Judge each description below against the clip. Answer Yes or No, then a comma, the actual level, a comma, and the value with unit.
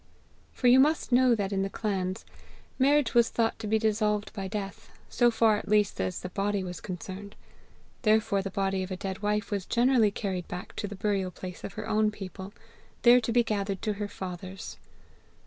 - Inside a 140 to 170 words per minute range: No, average, 200 wpm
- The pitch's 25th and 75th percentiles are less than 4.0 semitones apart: Yes, narrow, 2.6 semitones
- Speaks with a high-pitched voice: Yes, high, 205 Hz